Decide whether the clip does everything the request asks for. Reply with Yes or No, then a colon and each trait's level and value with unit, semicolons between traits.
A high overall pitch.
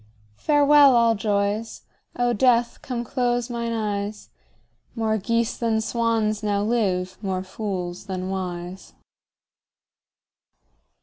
Yes: high, 220 Hz